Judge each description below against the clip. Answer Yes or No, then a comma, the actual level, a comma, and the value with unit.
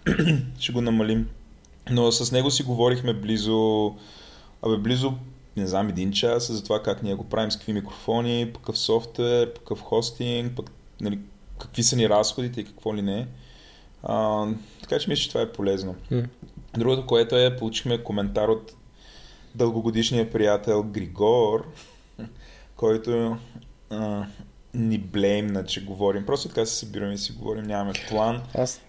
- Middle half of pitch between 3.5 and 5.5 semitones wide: No, average, 2.7 semitones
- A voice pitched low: Yes, low, 110 Hz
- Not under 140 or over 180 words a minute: Yes, average, 145 wpm